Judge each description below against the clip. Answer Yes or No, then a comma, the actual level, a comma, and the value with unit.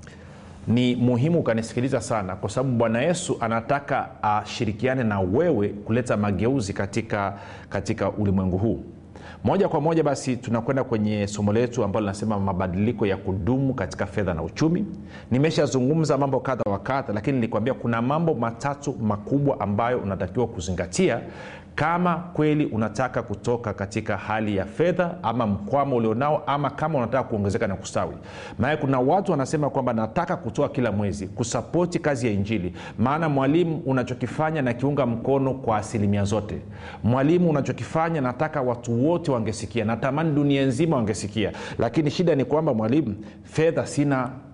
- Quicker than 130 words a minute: Yes, fast, 140 wpm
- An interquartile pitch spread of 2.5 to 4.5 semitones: No, average, 5.0 semitones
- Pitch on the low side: Yes, low, 120 Hz